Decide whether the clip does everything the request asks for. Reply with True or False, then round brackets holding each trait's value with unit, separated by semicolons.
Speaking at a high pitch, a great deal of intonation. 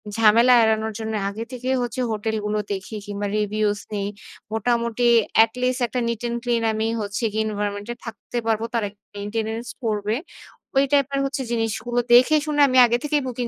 False (225 Hz; 2.5 semitones)